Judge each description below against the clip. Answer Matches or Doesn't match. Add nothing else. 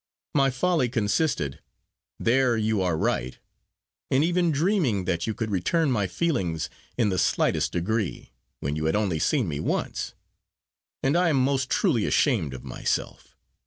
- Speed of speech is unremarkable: Matches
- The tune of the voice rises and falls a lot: Matches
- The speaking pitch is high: Doesn't match